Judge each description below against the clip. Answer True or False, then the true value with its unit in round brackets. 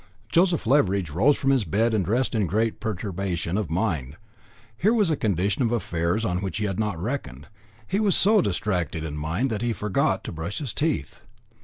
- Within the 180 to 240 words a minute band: True (195 wpm)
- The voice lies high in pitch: False (105 Hz)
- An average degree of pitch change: False (6.1 semitones)